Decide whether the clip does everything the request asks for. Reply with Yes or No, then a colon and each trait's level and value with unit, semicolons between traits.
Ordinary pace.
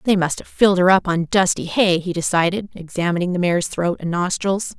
No: fast, 215 wpm